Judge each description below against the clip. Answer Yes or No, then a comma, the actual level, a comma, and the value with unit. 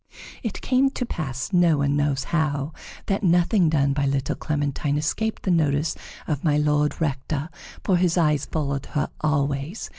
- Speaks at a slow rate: No, average, 160 wpm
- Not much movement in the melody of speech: No, average, 3.4 semitones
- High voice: No, medium, 150 Hz